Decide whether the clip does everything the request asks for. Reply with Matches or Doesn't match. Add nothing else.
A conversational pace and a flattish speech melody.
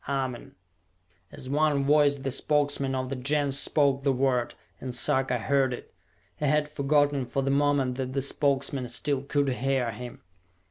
Matches